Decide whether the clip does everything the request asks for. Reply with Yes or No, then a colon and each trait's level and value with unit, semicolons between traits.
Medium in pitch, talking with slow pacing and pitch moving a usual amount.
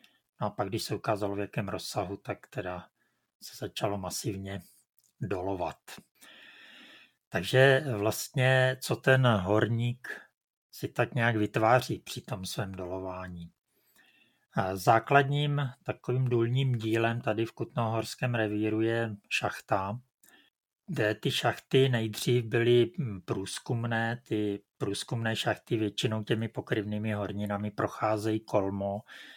No: low, 115 Hz; slow, 110 wpm; average, 3.1 semitones